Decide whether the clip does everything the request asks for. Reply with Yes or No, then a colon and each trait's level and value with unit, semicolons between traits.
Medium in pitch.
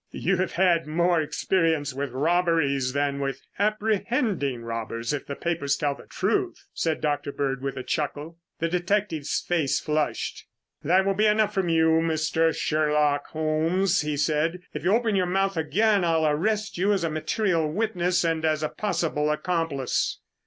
Yes: medium, 165 Hz